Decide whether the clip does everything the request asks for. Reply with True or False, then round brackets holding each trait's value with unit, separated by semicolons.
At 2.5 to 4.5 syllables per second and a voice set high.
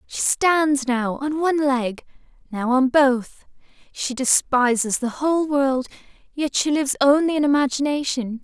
True (4.4 syllables/s; 270 Hz)